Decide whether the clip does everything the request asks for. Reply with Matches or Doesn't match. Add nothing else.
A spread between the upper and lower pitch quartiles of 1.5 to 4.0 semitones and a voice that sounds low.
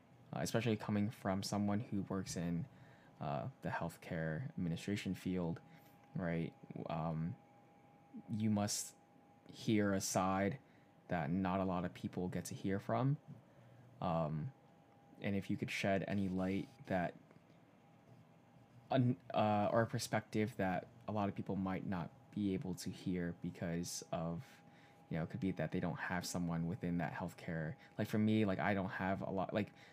Matches